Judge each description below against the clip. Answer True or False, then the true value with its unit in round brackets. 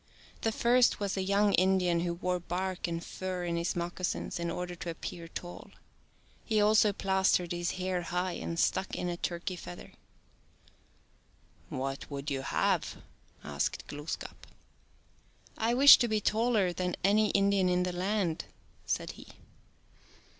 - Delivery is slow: False (160 wpm)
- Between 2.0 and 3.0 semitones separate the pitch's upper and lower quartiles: True (2.5 semitones)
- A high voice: False (180 Hz)